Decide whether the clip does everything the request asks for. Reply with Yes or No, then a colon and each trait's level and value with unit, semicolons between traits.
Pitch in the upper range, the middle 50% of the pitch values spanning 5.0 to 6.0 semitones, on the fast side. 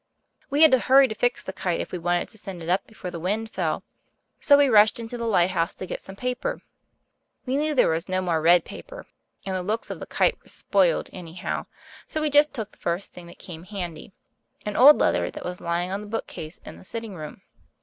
Yes: high, 195 Hz; average, 5.3 semitones; fast, 230 wpm